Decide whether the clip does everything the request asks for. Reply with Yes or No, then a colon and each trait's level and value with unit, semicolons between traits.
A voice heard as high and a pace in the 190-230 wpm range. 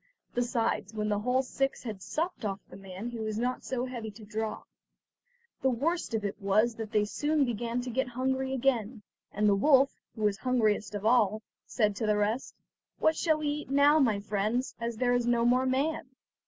Yes: high, 235 Hz; fast, 205 wpm